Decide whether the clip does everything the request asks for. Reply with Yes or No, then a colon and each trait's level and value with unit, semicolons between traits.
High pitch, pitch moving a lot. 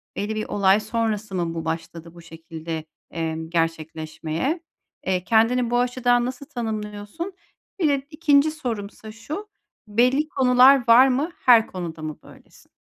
Yes: high, 220 Hz; wide, 7.1 semitones